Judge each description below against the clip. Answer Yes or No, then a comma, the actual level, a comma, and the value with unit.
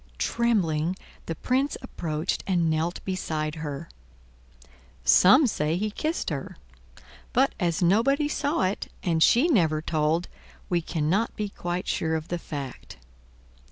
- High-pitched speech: No, medium, 175 Hz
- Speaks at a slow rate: Yes, slow, 130 wpm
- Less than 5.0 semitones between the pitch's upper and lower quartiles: No, wide, 5.4 semitones